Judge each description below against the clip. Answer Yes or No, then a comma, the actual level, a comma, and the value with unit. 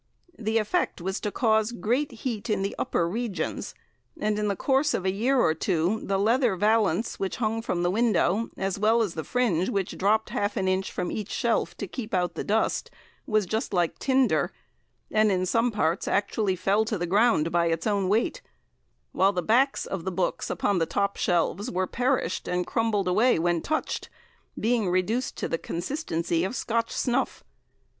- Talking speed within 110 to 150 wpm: No, average, 190 wpm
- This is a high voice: Yes, high, 205 Hz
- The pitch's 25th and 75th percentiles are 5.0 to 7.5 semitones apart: No, average, 4.0 semitones